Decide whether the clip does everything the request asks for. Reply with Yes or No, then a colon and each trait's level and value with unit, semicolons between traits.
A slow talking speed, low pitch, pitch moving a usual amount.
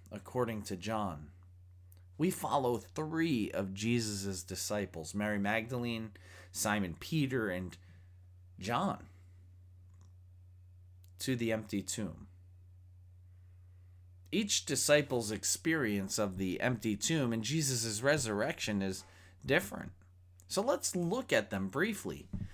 Yes: slow, 100 wpm; very low, 95 Hz; average, 3.9 semitones